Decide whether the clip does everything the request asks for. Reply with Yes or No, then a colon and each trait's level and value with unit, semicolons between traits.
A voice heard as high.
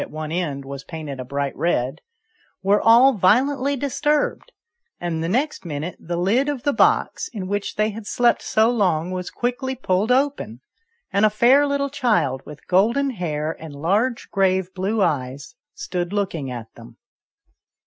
Yes: high, 195 Hz